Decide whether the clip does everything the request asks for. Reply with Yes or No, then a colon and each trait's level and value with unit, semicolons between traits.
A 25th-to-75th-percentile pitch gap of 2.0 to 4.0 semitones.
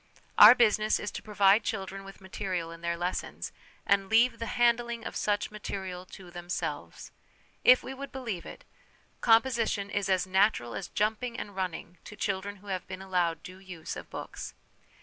Yes: average, 3.1 semitones